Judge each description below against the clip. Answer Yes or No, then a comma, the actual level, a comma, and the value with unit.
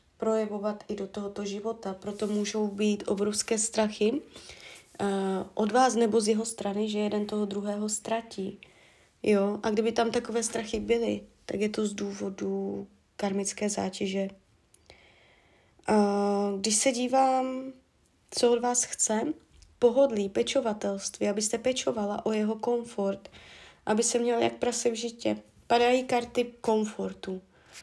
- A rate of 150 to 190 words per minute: No, average, 130 wpm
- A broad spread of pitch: No, narrow, 2.5 semitones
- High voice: Yes, high, 215 Hz